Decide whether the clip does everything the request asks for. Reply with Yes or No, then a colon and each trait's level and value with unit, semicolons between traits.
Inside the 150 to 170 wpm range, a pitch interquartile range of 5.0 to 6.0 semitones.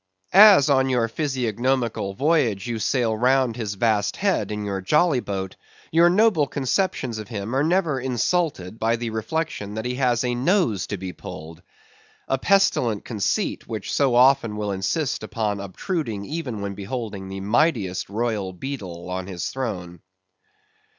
Yes: average, 155 wpm; average, 5.3 semitones